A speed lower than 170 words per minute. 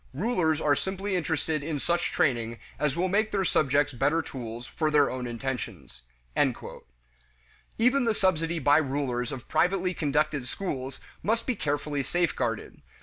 Yes: average, 145 wpm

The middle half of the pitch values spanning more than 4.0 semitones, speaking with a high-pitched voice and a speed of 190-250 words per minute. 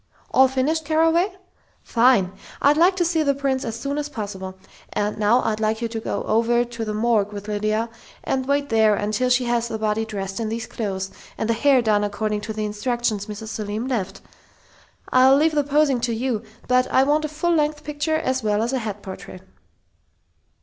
Yes: average, 4.6 semitones; high, 235 Hz; average, 200 wpm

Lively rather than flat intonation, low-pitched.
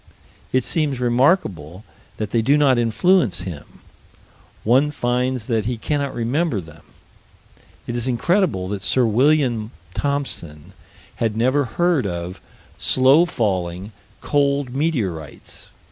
Yes: wide, 5.9 semitones; low, 120 Hz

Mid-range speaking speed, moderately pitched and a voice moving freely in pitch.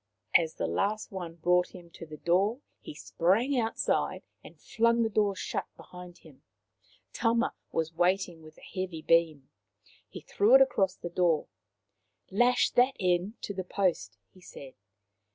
No: average, 160 wpm; medium, 180 Hz; average, 4.4 semitones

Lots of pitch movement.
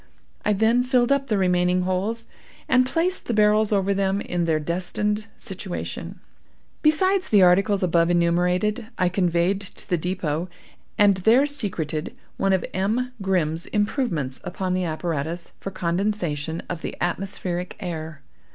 No: average, 3.4 semitones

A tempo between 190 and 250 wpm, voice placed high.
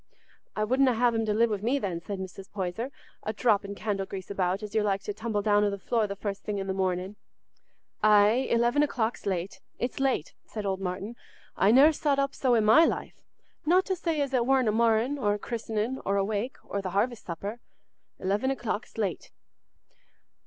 Yes: average, 200 wpm; high, 215 Hz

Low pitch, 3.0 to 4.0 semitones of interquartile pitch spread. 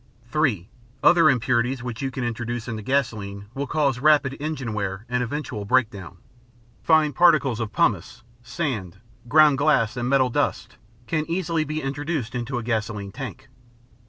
No: low, 125 Hz; average, 4.6 semitones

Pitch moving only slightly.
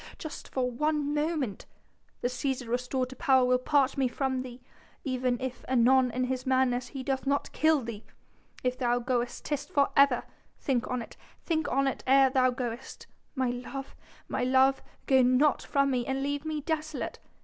Yes: narrow, 1.9 semitones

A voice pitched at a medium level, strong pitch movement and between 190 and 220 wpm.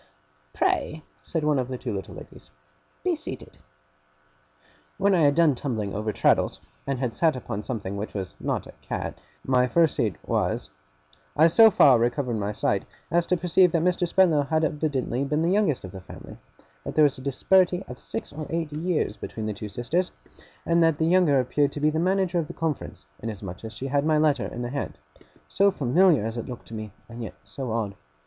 Yes: medium, 145 Hz; wide, 6.1 semitones; fast, 205 wpm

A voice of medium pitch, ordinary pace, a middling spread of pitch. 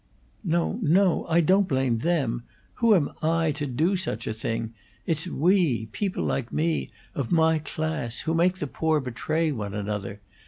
No: medium, 155 Hz; average, 165 wpm; wide, 6.1 semitones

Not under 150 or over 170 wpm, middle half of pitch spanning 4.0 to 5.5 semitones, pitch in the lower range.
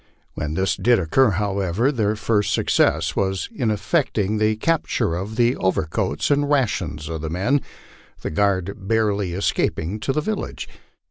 Yes: average, 155 wpm; average, 4.5 semitones; low, 105 Hz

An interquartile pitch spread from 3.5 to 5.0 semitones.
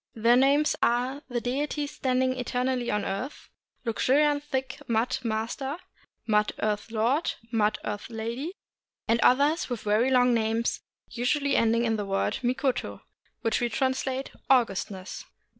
No: average, 3.0 semitones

